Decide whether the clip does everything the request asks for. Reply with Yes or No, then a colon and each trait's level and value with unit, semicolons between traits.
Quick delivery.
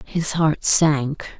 No: slow, 130 wpm